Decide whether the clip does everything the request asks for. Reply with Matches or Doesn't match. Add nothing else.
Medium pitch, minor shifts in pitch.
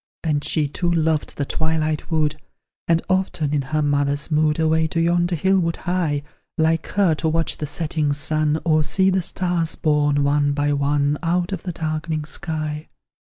Matches